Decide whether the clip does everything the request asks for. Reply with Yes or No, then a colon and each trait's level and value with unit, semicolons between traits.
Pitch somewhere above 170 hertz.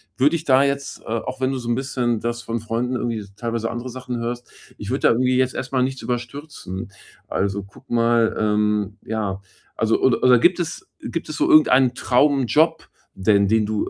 No: low, 120 Hz